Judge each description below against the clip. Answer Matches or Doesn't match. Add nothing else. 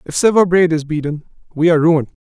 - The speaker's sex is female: Doesn't match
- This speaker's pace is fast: Matches